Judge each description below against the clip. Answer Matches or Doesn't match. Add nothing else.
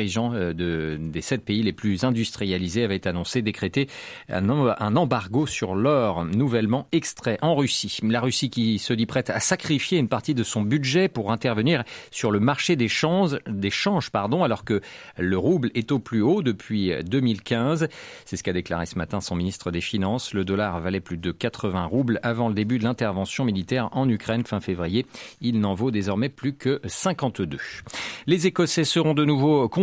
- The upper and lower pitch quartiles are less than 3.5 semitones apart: Doesn't match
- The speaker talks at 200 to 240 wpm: Doesn't match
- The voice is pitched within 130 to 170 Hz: Doesn't match